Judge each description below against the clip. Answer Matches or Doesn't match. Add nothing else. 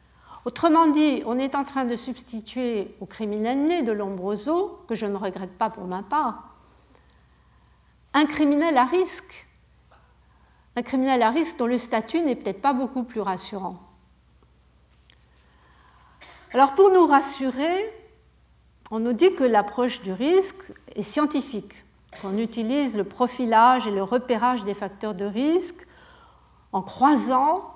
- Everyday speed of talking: Doesn't match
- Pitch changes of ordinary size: Doesn't match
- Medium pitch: Doesn't match